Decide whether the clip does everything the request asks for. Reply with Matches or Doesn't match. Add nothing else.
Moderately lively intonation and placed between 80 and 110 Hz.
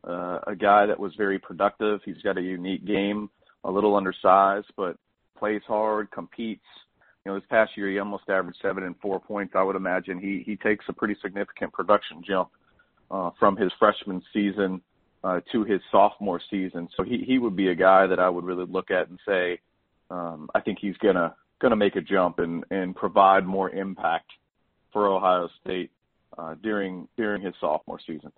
Doesn't match